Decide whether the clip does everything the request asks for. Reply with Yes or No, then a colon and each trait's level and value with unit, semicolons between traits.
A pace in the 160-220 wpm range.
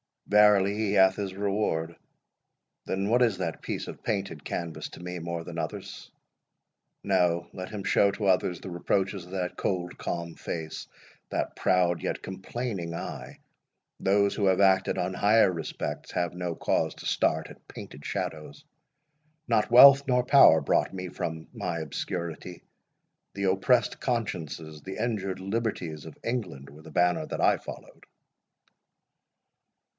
No: average, 150 wpm